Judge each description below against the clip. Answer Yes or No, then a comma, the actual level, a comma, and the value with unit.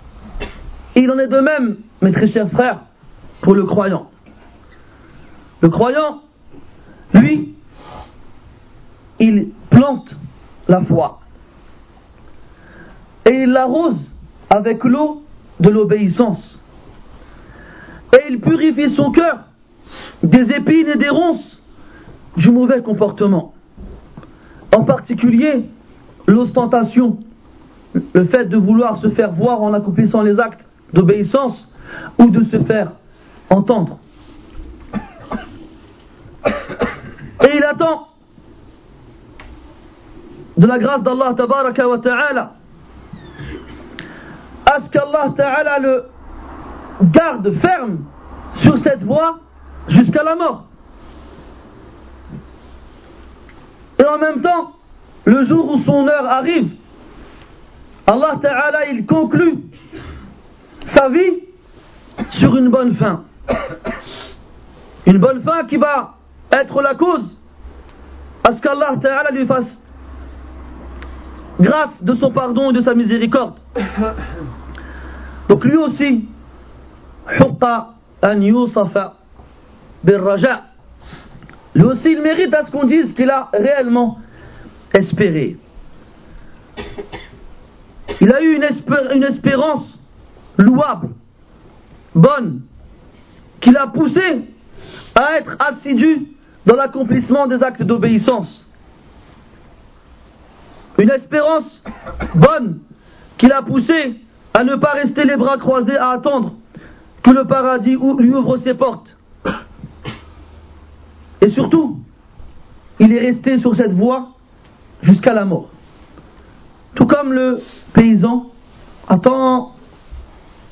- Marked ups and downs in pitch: Yes, wide, 6.1 semitones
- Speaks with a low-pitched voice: No, high, 245 Hz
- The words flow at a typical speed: No, slow, 100 wpm